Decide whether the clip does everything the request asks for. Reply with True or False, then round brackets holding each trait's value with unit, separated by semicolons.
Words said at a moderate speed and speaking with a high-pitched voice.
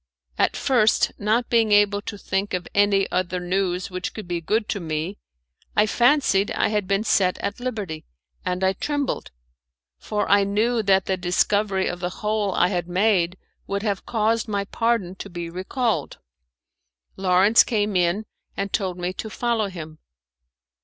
True (165 wpm; 200 Hz)